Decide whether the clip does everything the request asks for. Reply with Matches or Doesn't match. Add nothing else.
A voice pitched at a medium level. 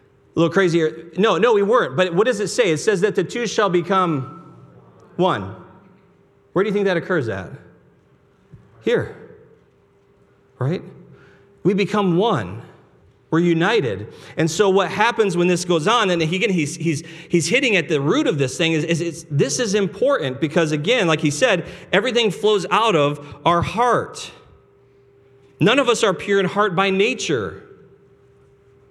Matches